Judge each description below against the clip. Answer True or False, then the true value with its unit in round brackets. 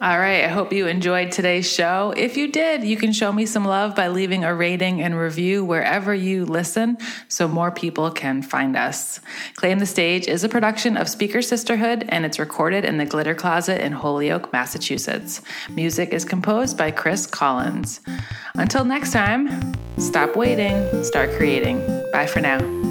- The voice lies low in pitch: False (185 Hz)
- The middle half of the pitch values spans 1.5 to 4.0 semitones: False (4.7 semitones)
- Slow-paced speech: False (175 wpm)